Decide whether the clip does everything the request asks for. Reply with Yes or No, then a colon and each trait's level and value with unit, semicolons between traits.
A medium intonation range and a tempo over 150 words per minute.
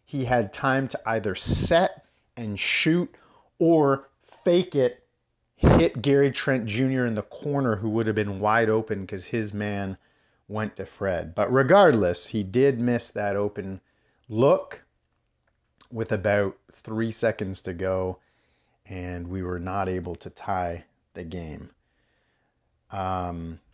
No: average, 4.9 semitones; slow, 135 wpm